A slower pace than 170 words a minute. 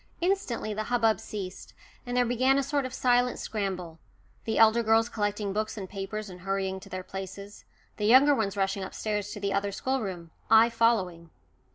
No: average, 180 wpm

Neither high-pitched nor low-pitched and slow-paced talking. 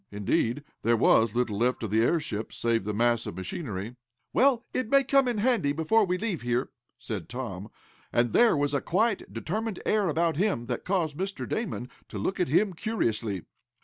No: medium, 145 Hz; average, 185 wpm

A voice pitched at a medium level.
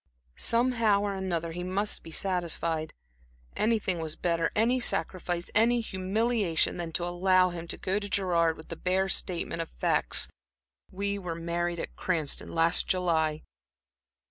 Yes: medium, 180 Hz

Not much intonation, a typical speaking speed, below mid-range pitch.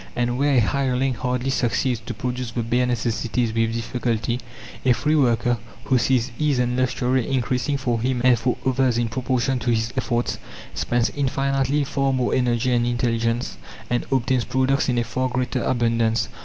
Yes: narrow, 1.8 semitones; average, 170 wpm; low, 125 Hz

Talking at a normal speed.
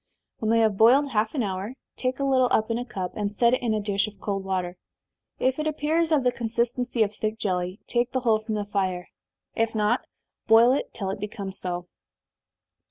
No: fast, 215 wpm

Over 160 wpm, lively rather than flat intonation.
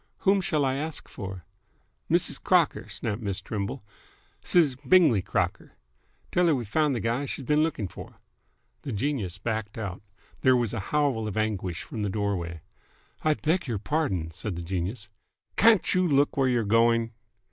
Yes: average, 170 wpm; wide, 6.4 semitones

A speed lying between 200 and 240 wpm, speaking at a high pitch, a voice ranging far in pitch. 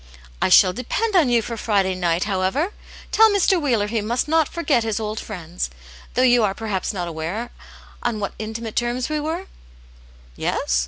No: average, 175 wpm; high, 225 Hz; wide, 5.7 semitones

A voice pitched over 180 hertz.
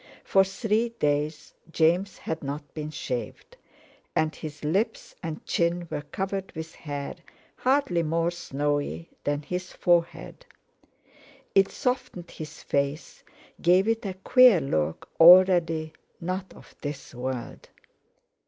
No: medium, 165 Hz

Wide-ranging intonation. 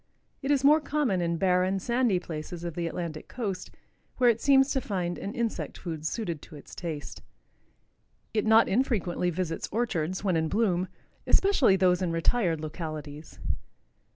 Yes: wide, 5.8 semitones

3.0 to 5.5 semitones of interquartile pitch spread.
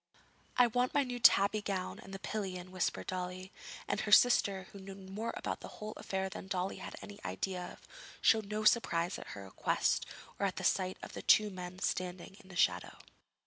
No: narrow, 2.5 semitones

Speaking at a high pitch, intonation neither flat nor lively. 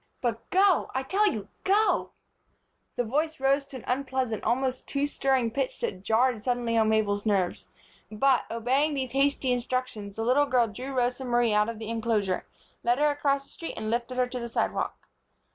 Yes: very high, 250 Hz; average, 3.4 semitones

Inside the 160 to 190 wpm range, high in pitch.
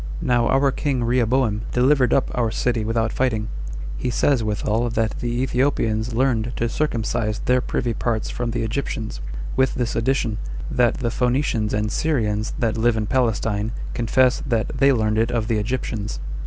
No: average, 170 wpm; low, 120 Hz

